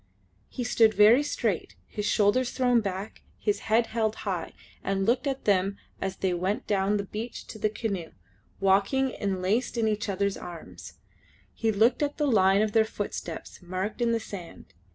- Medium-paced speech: Yes, average, 175 wpm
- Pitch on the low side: No, high, 210 Hz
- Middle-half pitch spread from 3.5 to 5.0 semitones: No, average, 3.0 semitones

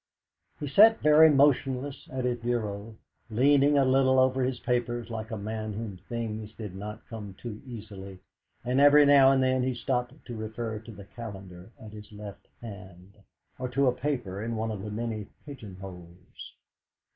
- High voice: No, low, 115 Hz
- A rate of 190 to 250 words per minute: No, average, 175 wpm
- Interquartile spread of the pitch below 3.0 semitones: No, average, 3.9 semitones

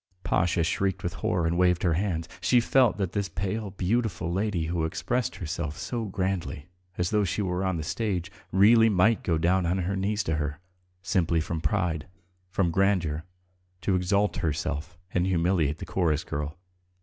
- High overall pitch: No, very low, 90 Hz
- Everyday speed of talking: Yes, average, 175 wpm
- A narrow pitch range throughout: No, average, 3.2 semitones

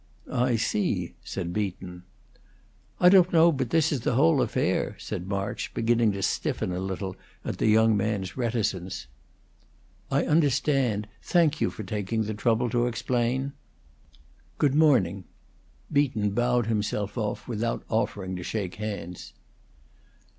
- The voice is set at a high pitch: No, low, 110 Hz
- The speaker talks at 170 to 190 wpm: No, slow, 135 wpm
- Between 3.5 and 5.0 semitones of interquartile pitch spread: Yes, average, 4.7 semitones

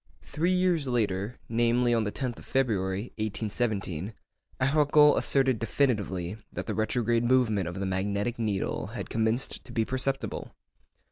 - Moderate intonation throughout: Yes, average, 4.1 semitones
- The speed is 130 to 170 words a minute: Yes, average, 140 wpm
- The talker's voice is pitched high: No, low, 115 Hz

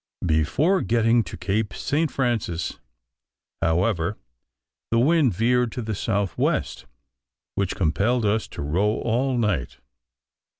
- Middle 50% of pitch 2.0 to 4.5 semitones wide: No, average, 4.9 semitones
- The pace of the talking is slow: Yes, slow, 120 wpm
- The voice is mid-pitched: No, low, 110 Hz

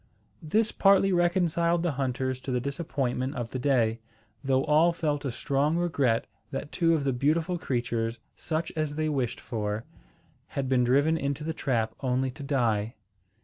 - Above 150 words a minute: Yes, average, 165 wpm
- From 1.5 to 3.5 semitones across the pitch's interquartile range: No, average, 4.3 semitones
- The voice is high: No, medium, 140 Hz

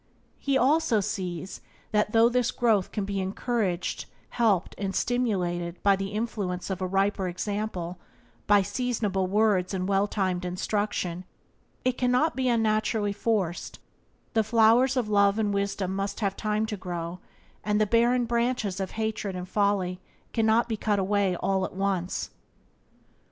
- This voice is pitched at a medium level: No, high, 205 Hz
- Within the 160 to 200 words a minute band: No, average, 150 wpm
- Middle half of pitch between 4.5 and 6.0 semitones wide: No, average, 2.9 semitones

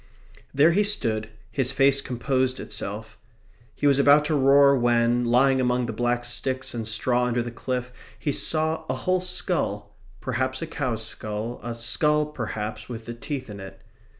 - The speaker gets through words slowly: No, average, 170 wpm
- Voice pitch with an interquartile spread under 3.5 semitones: Yes, average, 3.0 semitones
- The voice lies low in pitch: Yes, low, 125 Hz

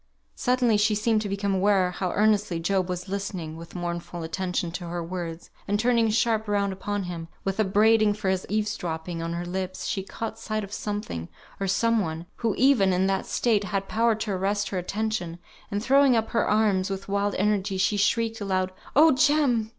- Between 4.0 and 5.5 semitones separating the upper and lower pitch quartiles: No, average, 3.0 semitones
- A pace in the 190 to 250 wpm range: Yes, average, 195 wpm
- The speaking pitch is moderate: No, high, 200 Hz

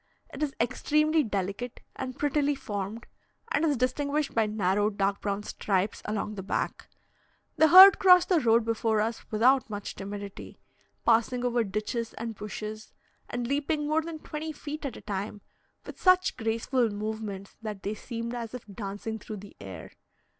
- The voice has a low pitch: No, high, 230 Hz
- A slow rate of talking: No, average, 160 wpm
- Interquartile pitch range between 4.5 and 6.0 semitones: Yes, average, 5.3 semitones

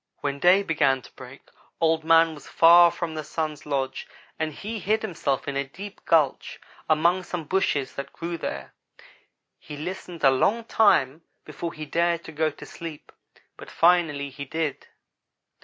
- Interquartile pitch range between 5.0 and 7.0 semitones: No, average, 3.4 semitones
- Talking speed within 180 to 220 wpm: No, average, 165 wpm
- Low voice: No, medium, 160 Hz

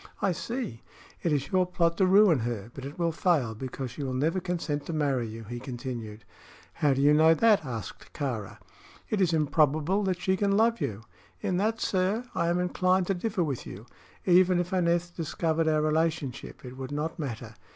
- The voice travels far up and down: Yes, wide, 5.7 semitones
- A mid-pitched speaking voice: Yes, medium, 160 Hz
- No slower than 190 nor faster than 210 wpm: Yes, average, 195 wpm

